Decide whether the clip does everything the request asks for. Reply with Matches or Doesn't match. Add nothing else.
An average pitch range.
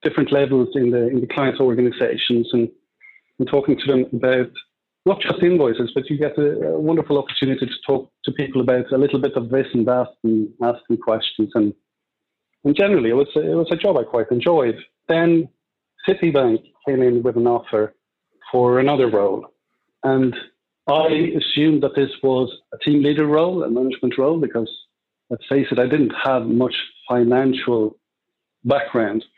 Matches